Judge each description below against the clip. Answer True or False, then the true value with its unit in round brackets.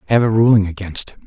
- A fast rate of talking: True (240 wpm)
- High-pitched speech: False (105 Hz)